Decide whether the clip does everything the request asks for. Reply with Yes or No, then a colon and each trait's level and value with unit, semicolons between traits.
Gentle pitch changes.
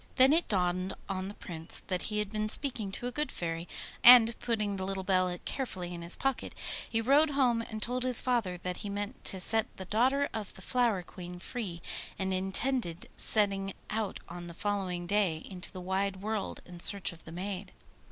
No: average, 4.0 semitones